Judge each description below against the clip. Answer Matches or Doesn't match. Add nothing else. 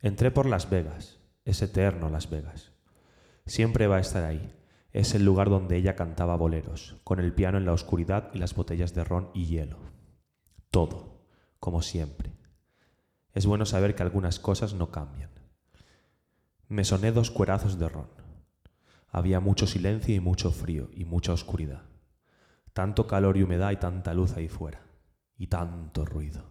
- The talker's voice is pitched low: Matches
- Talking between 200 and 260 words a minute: Doesn't match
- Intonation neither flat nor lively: Matches